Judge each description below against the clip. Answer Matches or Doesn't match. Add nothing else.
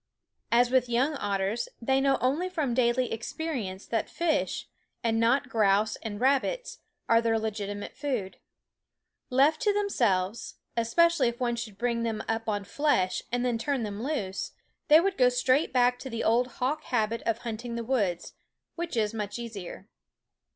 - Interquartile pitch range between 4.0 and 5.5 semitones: Doesn't match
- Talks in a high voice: Matches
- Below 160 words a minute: Doesn't match